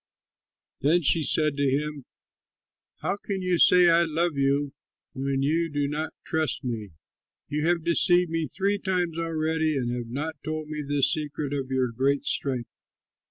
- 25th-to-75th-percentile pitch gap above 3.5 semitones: No, average, 3.2 semitones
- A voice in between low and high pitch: Yes, medium, 150 Hz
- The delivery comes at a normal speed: Yes, average, 160 wpm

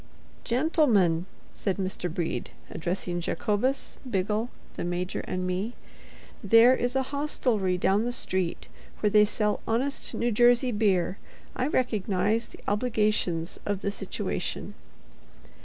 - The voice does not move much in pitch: No, average, 4.7 semitones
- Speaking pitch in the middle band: No, high, 210 Hz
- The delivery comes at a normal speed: No, slow, 125 wpm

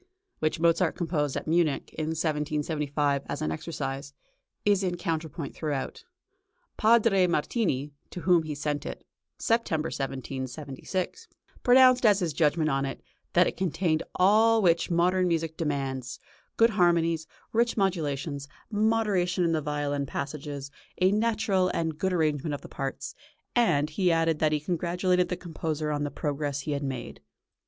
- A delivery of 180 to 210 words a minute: No, average, 145 wpm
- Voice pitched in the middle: Yes, medium, 160 Hz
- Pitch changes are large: No, average, 3.9 semitones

